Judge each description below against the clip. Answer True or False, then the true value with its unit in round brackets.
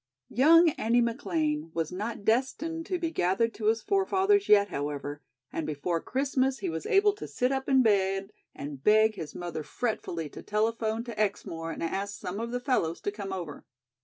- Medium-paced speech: True (185 wpm)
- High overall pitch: True (215 Hz)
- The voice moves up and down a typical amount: False (7.2 semitones)